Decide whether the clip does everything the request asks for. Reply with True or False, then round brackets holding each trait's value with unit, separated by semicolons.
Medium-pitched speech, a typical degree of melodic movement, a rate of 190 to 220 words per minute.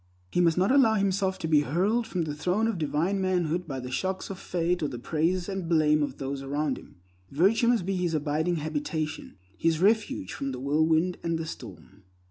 True (165 Hz; 4.0 semitones; 205 wpm)